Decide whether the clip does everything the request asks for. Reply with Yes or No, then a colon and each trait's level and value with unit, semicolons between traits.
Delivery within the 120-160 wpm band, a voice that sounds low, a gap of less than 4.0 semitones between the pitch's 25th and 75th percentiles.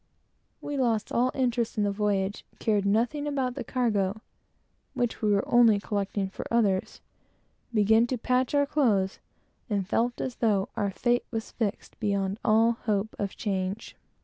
No: average, 150 wpm; high, 220 Hz; average, 3.2 semitones